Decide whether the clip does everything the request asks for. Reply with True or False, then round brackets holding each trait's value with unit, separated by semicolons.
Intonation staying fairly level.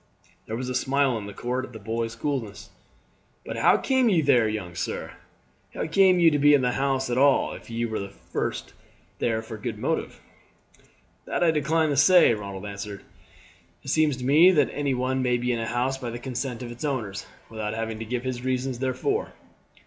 False (3.8 semitones)